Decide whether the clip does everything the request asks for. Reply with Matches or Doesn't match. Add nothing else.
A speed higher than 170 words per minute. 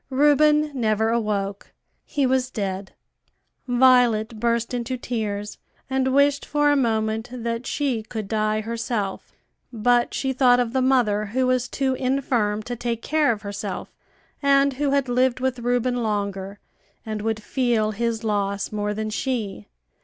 Doesn't match